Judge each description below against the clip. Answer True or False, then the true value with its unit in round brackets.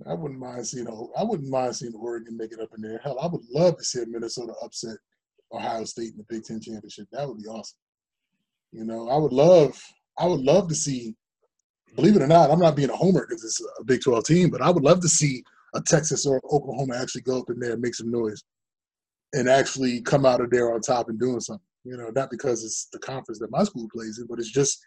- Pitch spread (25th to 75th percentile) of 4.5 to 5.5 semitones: False (4.0 semitones)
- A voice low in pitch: True (125 Hz)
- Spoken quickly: True (260 wpm)